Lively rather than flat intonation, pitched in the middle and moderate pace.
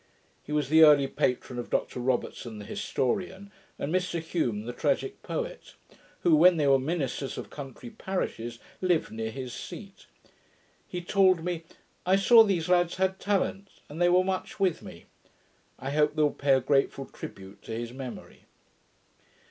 Yes: wide, 5.9 semitones; medium, 155 Hz; average, 170 wpm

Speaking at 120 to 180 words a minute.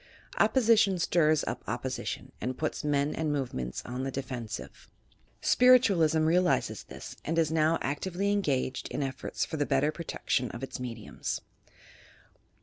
Yes: average, 145 wpm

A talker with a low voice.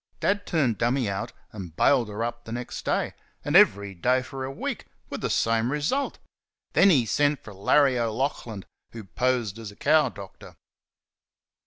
Yes: low, 120 Hz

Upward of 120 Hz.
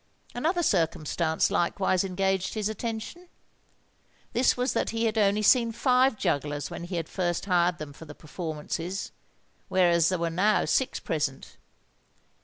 Yes: medium, 185 Hz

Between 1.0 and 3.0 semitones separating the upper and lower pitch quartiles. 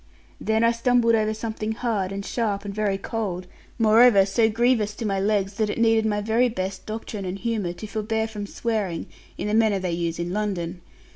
Yes: narrow, 2.4 semitones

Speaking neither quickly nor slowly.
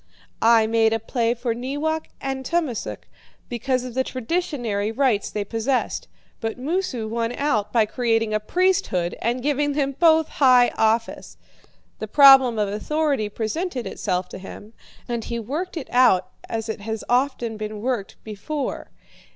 Yes: average, 150 wpm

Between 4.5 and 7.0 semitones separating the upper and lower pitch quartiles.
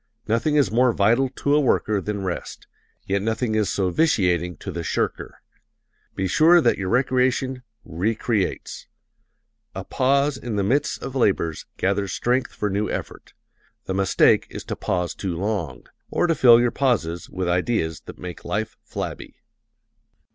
Yes: wide, 5.4 semitones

